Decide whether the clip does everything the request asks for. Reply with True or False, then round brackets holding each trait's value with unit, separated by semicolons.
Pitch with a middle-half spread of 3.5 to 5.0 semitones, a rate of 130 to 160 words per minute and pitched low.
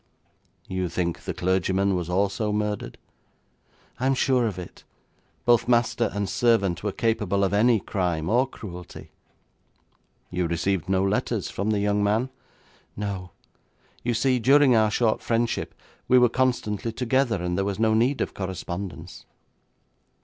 True (3.9 semitones; 145 wpm; 105 Hz)